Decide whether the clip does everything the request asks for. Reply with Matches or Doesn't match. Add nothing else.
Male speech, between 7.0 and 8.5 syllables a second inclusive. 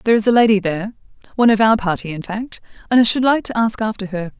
Doesn't match